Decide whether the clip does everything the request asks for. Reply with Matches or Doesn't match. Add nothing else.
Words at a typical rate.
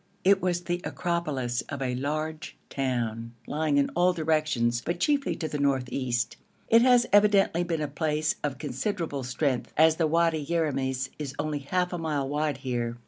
Matches